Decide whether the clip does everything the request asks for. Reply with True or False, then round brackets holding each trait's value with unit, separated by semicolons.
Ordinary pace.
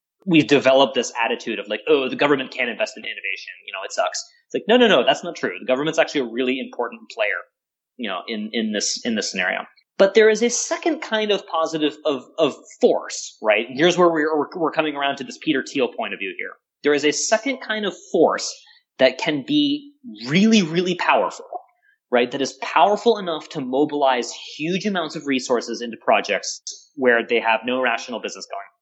False (210 wpm)